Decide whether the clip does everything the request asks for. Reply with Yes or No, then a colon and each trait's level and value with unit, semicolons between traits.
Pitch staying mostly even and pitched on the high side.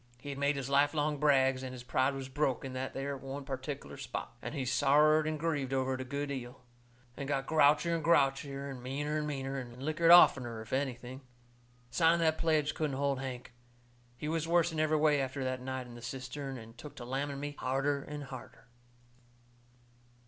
No: narrow, 2.2 semitones; medium, 140 Hz